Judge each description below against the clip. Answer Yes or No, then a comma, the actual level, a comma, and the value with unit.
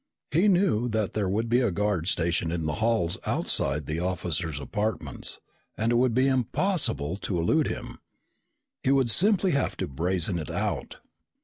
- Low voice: Yes, low, 105 Hz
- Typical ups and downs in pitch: No, wide, 7.0 semitones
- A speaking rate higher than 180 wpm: No, average, 170 wpm